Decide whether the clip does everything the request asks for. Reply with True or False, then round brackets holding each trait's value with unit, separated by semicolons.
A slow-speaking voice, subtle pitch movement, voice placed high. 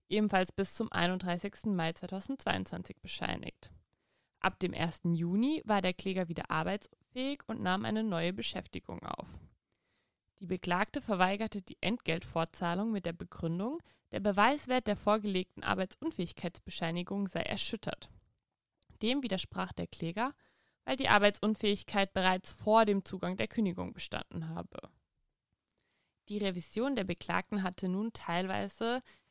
False (120 wpm; 3.5 semitones; 195 Hz)